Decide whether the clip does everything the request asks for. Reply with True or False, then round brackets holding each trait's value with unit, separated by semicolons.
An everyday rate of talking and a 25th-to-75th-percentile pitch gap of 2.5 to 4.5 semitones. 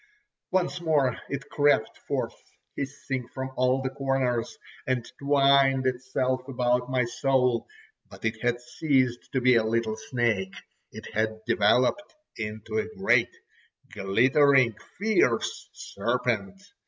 False (120 wpm; 2.8 semitones)